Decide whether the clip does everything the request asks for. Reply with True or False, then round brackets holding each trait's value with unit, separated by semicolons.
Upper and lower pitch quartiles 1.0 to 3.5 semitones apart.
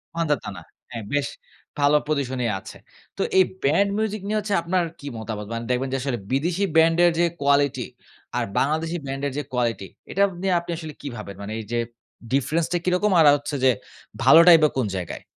False (5.0 semitones)